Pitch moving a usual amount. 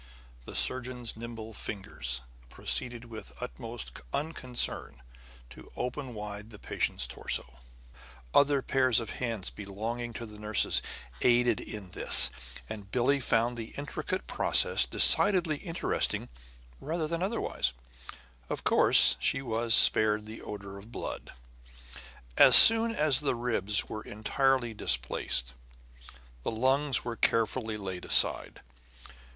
Yes: average, 3.9 semitones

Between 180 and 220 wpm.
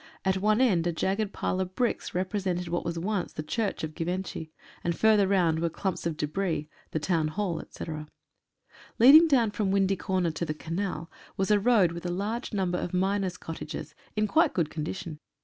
Yes: average, 195 wpm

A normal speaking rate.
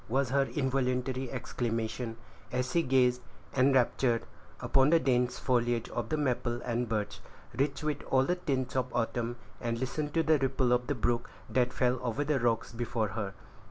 Yes: average, 170 wpm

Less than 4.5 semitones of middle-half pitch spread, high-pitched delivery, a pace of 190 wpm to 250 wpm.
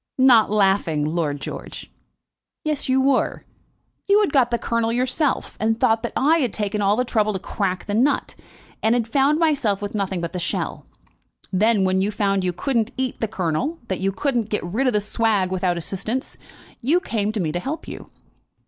No: average, 5.1 semitones; high, 215 Hz; average, 195 wpm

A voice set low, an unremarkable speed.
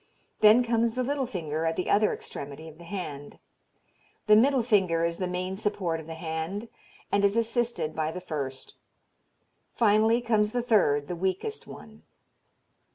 No: high, 190 Hz; average, 160 wpm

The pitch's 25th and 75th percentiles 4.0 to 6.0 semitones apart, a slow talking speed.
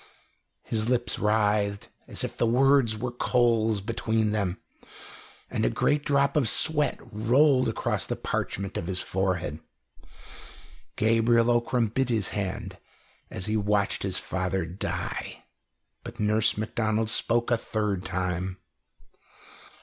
No: average, 3.3 semitones; slow, 125 wpm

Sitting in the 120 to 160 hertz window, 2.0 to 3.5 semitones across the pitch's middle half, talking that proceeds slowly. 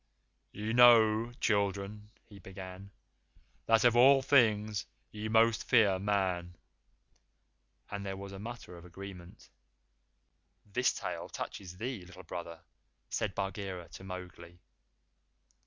No: low, 100 Hz; average, 3.0 semitones; slow, 115 wpm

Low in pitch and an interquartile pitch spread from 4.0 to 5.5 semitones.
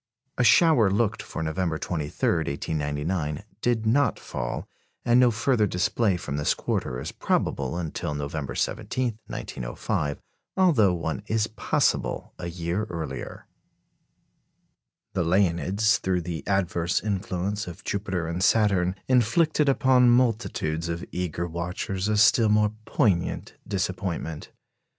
Yes: very low, 95 Hz; average, 4.8 semitones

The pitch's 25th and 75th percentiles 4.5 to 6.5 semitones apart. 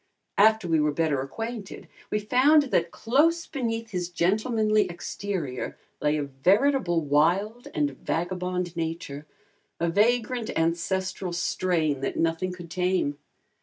Yes: average, 5.1 semitones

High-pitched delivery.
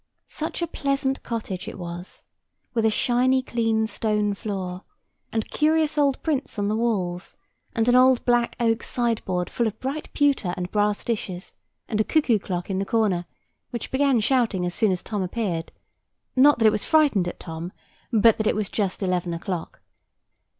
Yes: high, 220 Hz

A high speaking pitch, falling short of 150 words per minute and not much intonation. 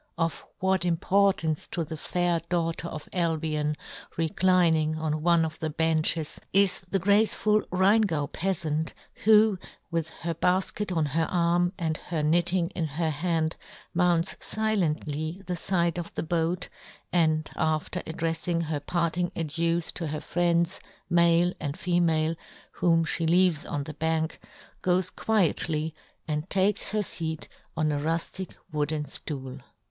No: medium, 165 Hz; average, 140 wpm; narrow, 2.2 semitones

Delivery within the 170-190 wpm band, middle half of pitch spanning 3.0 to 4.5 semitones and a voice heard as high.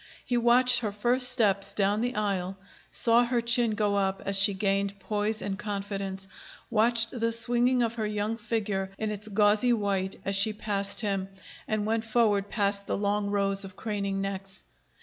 No: average, 175 wpm; narrow, 2.6 semitones; high, 210 Hz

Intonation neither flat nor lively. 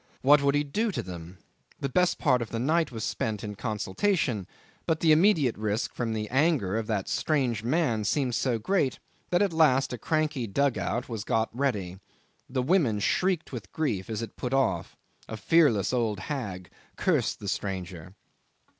No: wide, 6.0 semitones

